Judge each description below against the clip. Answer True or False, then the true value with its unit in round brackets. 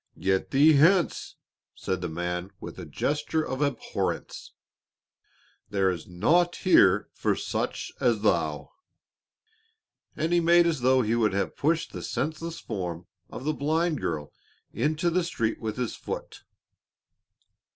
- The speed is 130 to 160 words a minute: True (140 wpm)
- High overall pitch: False (130 Hz)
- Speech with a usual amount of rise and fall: False (9.0 semitones)